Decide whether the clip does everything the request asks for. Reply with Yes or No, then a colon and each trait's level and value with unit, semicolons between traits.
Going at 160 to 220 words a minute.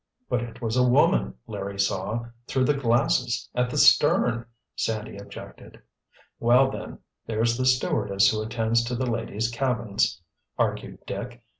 No: average, 140 wpm